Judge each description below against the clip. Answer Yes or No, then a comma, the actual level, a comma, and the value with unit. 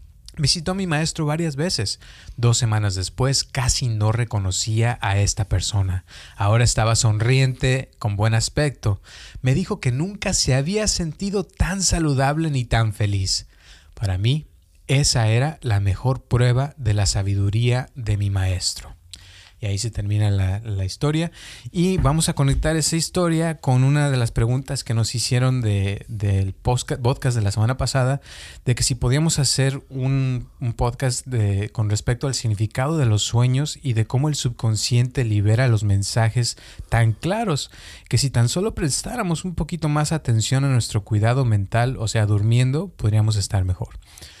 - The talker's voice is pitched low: Yes, low, 120 Hz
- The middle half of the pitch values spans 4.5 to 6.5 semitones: Yes, average, 4.8 semitones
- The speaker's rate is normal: Yes, average, 160 wpm